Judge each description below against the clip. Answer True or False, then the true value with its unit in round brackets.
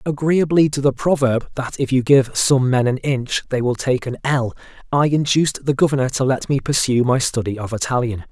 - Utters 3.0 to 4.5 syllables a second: False (5.3 syllables/s)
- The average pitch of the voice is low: True (130 Hz)